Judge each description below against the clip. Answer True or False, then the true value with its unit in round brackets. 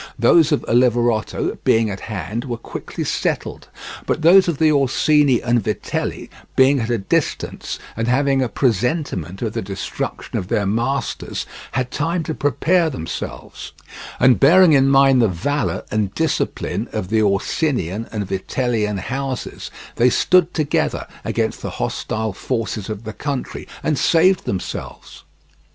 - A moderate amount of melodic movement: True (4.9 semitones)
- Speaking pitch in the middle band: False (125 Hz)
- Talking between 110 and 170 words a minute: True (145 wpm)